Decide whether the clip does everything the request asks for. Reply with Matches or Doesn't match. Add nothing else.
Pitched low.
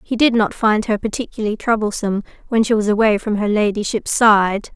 Doesn't match